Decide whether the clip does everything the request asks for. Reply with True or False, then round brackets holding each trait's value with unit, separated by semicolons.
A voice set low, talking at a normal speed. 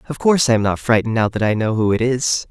False (115 Hz; 310 wpm)